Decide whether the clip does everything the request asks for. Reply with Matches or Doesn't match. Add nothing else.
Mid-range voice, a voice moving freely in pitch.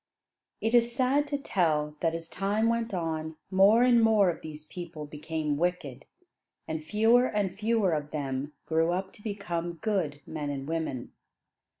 Matches